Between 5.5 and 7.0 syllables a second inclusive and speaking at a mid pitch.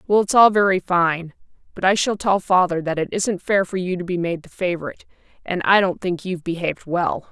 Yes: 5.7 syllables/s; medium, 180 Hz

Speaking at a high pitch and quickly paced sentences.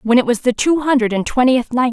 Yes: high, 245 Hz; fast, 280 wpm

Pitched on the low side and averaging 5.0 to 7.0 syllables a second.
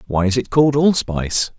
Yes: low, 120 Hz; 5.7 syllables/s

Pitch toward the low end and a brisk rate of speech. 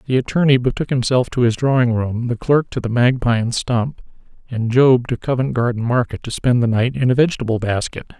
Yes: low, 125 Hz; fast, 210 wpm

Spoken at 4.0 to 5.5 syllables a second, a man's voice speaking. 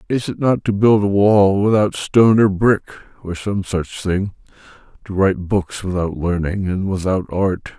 Yes: 4.5 syllables/s; male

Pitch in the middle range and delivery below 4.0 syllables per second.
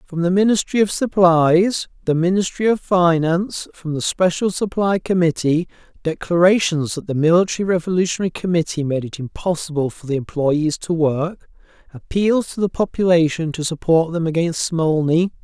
No: medium, 170 Hz; 5.1 syllables/s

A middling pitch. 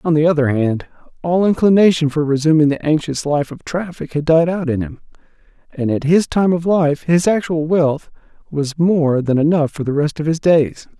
Yes: medium, 155 Hz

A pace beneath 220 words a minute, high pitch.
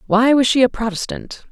Yes: average, 200 wpm; high, 240 Hz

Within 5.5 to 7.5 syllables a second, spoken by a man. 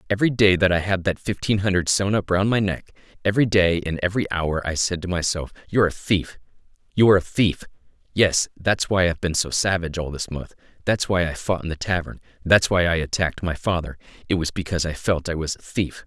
Yes: 6.0 syllables/s; male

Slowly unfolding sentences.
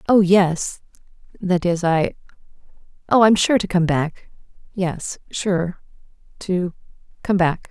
Yes: slow, 70 wpm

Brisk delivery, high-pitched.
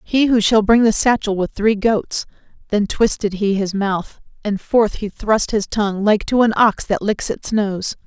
Yes: fast, 210 wpm; high, 210 Hz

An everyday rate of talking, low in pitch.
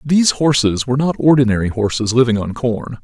Yes: average, 180 wpm; low, 125 Hz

